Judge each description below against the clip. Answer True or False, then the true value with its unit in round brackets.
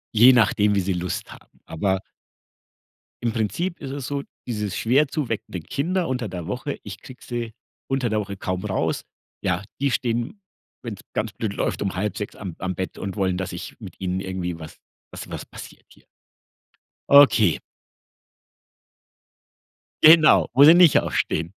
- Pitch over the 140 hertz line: False (110 Hz)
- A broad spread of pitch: True (6.1 semitones)